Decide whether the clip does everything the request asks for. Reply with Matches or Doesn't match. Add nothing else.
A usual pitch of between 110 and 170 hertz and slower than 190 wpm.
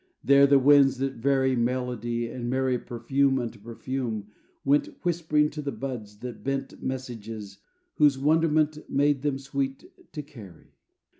Matches